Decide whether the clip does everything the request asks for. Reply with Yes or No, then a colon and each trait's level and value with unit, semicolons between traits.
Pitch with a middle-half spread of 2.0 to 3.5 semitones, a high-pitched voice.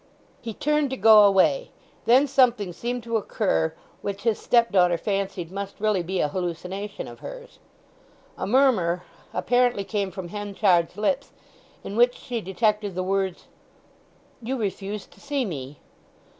No: average, 4.3 semitones; high, 205 Hz